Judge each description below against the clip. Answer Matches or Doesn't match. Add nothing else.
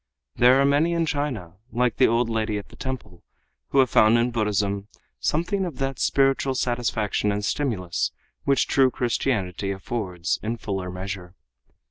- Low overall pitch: Matches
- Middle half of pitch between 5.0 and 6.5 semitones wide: Matches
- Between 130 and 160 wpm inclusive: Matches